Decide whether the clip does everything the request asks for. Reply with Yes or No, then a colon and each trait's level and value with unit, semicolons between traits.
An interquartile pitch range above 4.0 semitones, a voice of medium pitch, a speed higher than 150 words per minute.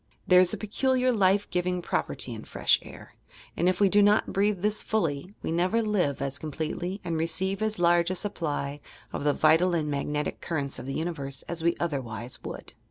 Yes: average, 4.9 semitones; medium, 175 Hz; average, 200 wpm